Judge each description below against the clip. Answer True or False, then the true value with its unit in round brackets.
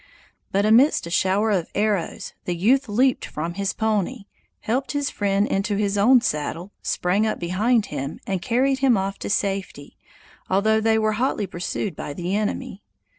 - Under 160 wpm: False (170 wpm)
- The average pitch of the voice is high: True (205 Hz)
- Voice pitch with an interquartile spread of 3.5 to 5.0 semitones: False (2.9 semitones)